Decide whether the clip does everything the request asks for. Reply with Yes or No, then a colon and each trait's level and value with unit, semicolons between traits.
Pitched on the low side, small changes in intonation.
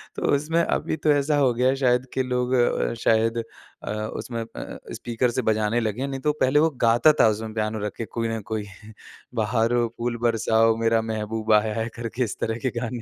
Yes: low, 115 Hz; narrow, 2.2 semitones